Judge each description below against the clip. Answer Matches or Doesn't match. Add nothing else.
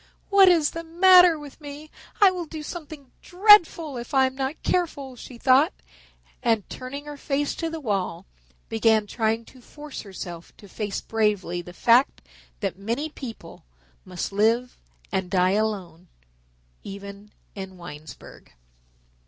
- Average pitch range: Doesn't match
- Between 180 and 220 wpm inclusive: Doesn't match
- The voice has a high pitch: Matches